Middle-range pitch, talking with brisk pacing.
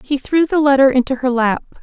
No: very high, 265 Hz; fast, 230 wpm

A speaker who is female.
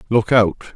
No: male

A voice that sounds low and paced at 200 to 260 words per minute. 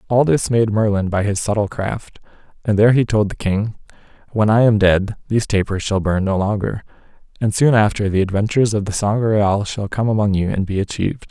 Yes: low, 105 Hz; fast, 205 wpm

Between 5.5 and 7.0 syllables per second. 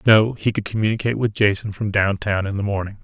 Yes: 6.2 syllables/s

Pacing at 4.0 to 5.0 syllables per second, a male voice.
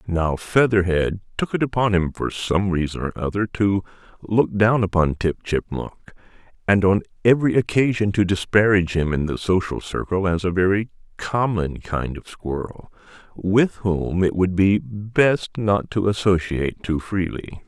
Yes: 4.5 syllables/s; male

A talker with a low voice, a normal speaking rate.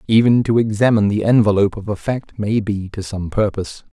Yes: low, 105 Hz; average, 195 wpm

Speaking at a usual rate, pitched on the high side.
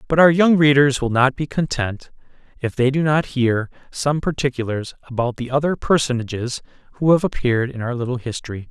No: average, 180 wpm; low, 135 Hz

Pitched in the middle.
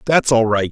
No: low, 120 Hz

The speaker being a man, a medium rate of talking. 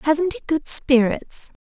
No: female; average, 150 wpm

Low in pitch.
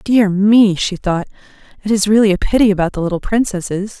No: high, 200 Hz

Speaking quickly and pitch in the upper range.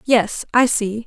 No: average, 170 wpm; high, 230 Hz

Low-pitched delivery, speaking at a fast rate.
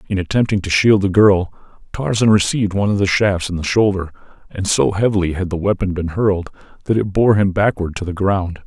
Yes: very low, 95 Hz; fast, 215 wpm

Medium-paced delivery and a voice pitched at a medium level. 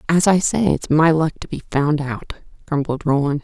No: fast, 210 wpm; medium, 155 Hz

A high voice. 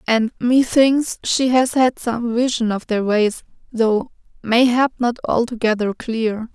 Yes: high, 235 Hz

